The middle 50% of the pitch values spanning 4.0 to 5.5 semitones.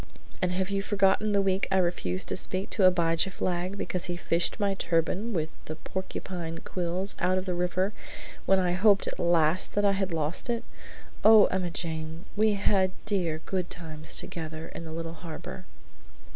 No: average, 2.7 semitones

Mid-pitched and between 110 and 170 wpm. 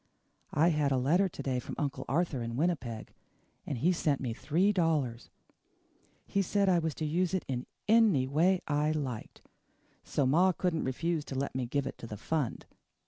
No: medium, 150 Hz; average, 185 wpm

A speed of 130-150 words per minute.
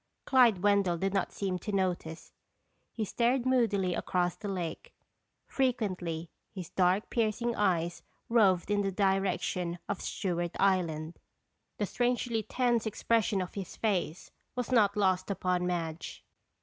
Yes: slow, 135 wpm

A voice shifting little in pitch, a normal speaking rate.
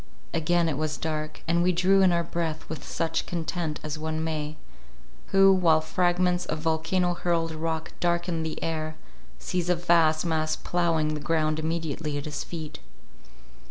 Yes: narrow, 1.8 semitones; average, 160 wpm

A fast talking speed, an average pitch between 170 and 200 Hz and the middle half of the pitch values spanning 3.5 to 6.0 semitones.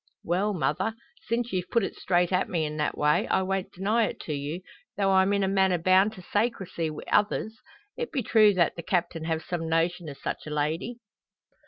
Yes: fast, 210 wpm; medium, 185 Hz; average, 3.9 semitones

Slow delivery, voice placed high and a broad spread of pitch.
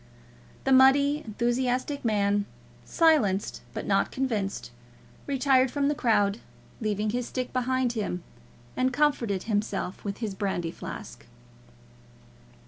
No: slow, 115 wpm; high, 240 Hz; average, 4.5 semitones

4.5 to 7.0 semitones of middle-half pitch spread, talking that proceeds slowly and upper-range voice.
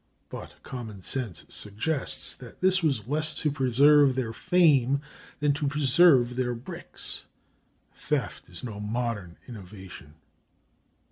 No: average, 4.8 semitones; slow, 120 wpm; low, 130 Hz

